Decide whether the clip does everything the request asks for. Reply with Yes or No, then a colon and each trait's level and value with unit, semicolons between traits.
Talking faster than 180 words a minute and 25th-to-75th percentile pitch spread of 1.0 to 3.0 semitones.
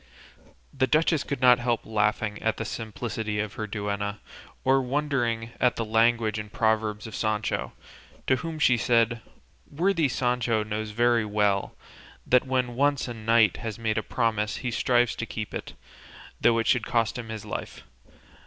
No: average, 165 wpm; narrow, 2.4 semitones